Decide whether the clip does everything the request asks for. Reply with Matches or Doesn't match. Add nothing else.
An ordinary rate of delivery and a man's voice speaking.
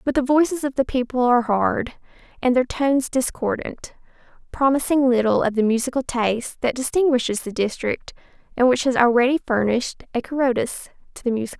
Doesn't match